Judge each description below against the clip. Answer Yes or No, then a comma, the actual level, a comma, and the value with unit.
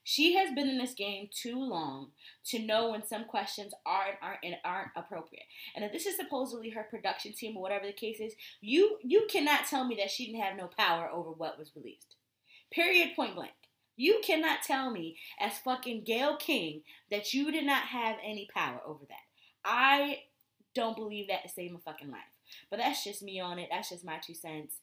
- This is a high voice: Yes, high, 220 Hz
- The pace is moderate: No, fast, 210 wpm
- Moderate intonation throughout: No, wide, 6.3 semitones